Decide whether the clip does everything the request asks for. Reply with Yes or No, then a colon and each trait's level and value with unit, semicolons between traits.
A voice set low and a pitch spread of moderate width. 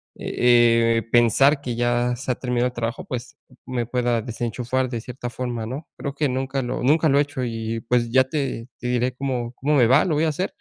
No: low, 125 Hz; narrow, 2.1 semitones